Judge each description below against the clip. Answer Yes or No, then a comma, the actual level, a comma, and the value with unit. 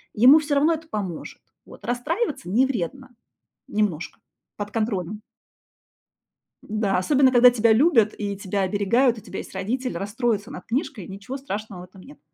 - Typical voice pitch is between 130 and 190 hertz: No, high, 220 Hz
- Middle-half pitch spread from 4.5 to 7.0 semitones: Yes, average, 4.8 semitones